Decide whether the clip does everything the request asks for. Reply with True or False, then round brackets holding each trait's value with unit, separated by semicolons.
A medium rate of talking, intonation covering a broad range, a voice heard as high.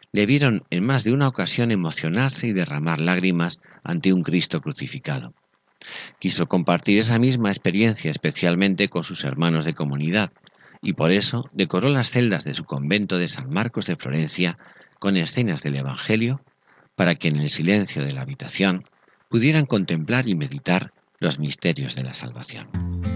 False (160 wpm; 6.0 semitones; 95 Hz)